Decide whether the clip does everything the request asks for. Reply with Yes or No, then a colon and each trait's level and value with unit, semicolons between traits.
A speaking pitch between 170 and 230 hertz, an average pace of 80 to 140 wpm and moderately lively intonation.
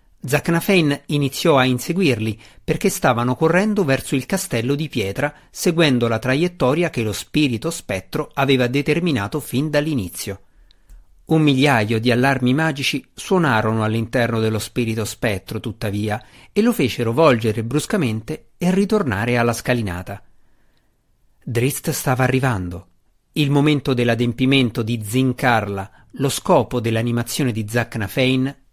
No: low, 130 Hz; slow, 115 wpm; average, 4.7 semitones